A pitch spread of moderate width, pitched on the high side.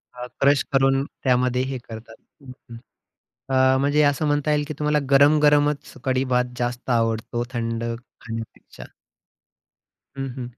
No: average, 3.0 semitones; low, 130 Hz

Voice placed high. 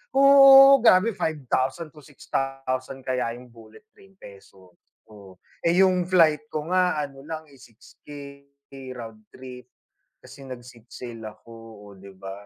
No: low, 130 Hz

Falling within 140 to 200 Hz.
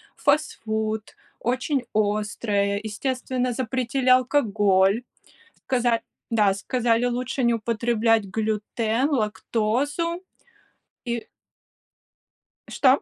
No: high, 235 Hz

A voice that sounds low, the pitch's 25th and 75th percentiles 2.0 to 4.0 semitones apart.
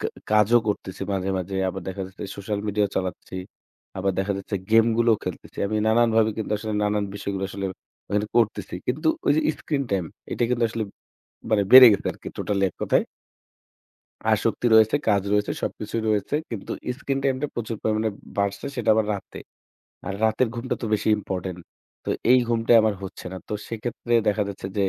Yes: low, 105 Hz; narrow, 2.6 semitones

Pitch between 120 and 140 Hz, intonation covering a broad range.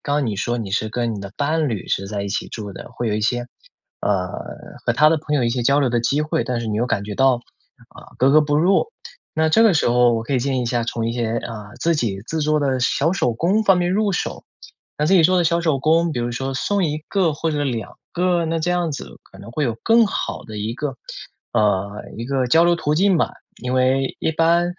Yes: low, 135 Hz; wide, 5.7 semitones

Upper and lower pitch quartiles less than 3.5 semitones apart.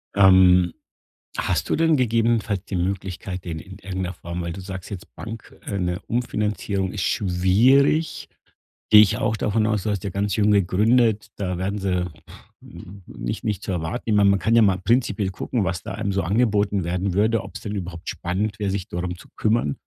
Yes: average, 2.8 semitones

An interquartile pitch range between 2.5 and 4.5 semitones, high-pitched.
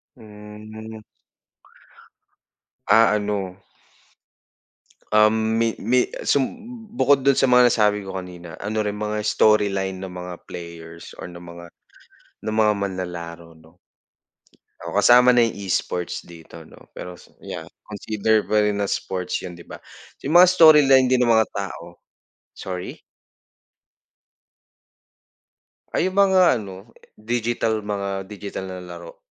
No: average, 3.7 semitones; low, 105 Hz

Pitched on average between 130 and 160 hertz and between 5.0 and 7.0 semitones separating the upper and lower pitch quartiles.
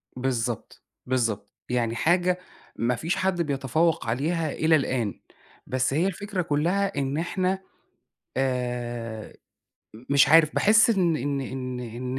Yes: medium, 140 Hz; wide, 5.6 semitones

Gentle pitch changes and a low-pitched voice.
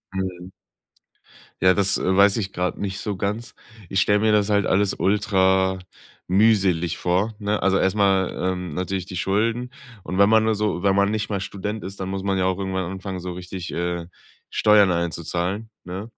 Yes: narrow, 1.9 semitones; very low, 95 Hz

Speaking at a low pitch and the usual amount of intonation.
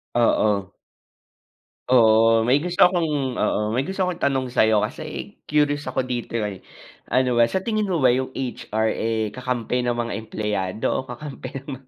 Yes: low, 125 Hz; average, 3.7 semitones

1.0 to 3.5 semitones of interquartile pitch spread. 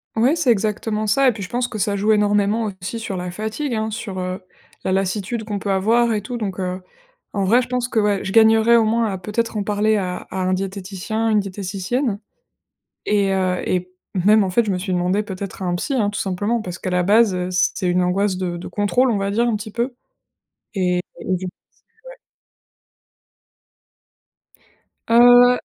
Yes: average, 3.2 semitones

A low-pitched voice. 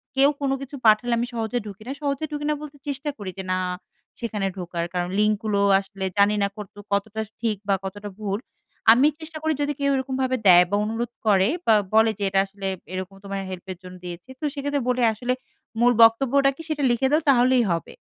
No: high, 220 Hz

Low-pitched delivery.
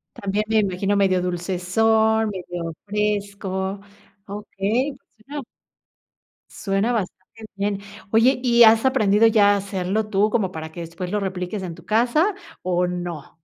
No: high, 200 Hz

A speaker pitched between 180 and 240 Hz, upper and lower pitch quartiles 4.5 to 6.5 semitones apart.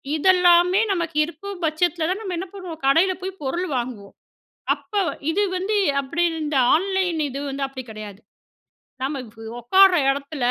No: very high, 335 Hz; average, 5.1 semitones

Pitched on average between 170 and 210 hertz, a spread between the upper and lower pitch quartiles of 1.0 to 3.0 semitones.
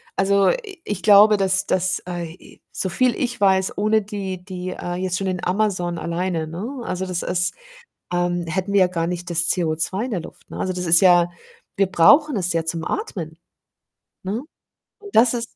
Yes: medium, 185 Hz; narrow, 2.6 semitones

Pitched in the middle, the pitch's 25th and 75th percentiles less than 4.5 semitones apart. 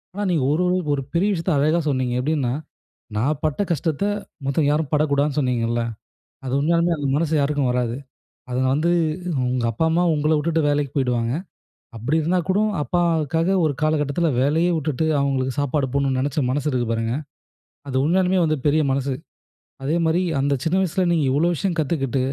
Yes: medium, 145 Hz; average, 3.5 semitones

